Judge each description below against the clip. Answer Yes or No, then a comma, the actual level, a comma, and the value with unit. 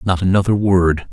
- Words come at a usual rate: Yes, average, 160 wpm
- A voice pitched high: No, very low, 95 Hz